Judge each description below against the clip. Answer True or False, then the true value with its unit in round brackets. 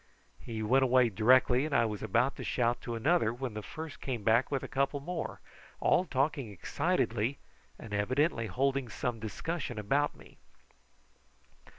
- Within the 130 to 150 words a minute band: False (165 wpm)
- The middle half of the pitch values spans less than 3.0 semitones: False (3.6 semitones)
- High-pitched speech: False (125 Hz)